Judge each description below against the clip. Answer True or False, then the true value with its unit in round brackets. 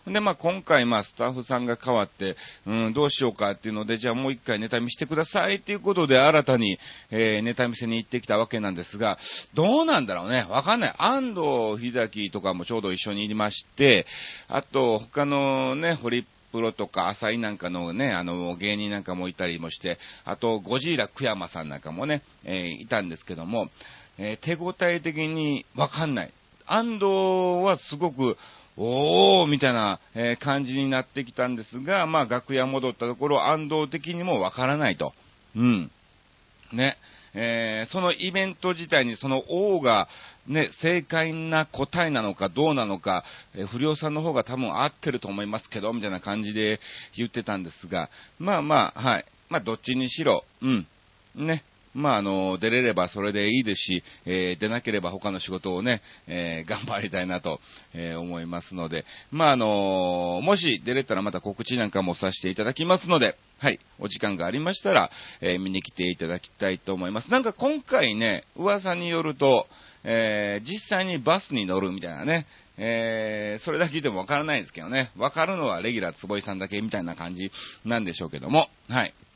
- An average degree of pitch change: False (7.4 semitones)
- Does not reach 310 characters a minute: False (375 characters per minute)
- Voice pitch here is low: True (115 Hz)